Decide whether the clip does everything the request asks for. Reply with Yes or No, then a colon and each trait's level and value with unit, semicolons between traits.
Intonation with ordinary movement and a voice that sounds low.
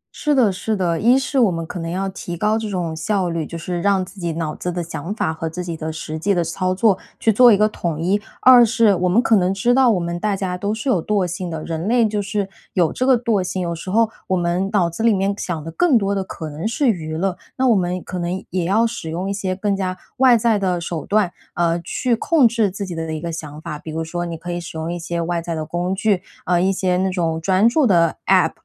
No: average, 3.7 semitones; medium, 185 Hz